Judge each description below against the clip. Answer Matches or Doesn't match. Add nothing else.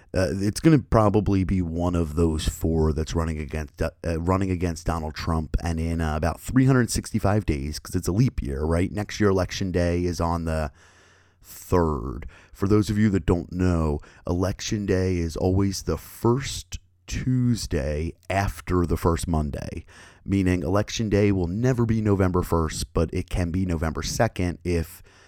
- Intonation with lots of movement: Doesn't match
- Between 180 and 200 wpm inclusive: Doesn't match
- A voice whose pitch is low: Matches